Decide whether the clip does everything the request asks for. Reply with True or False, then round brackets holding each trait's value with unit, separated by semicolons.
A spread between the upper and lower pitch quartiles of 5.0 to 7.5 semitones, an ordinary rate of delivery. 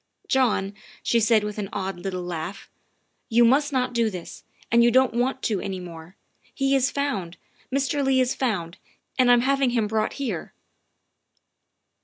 True (5.3 semitones; 175 wpm)